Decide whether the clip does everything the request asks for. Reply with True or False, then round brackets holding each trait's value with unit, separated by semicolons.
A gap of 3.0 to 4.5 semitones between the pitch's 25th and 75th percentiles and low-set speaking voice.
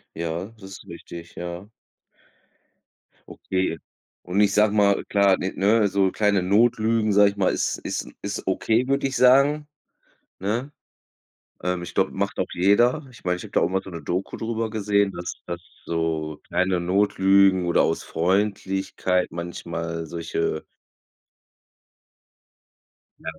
True (3.3 semitones; 95 Hz)